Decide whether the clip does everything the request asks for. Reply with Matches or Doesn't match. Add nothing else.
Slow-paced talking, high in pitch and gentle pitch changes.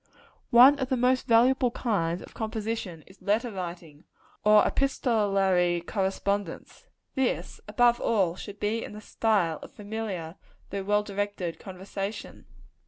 Doesn't match